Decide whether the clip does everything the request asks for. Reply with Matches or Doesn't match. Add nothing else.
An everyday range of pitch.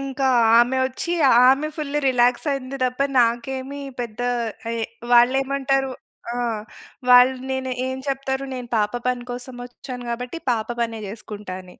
Doesn't match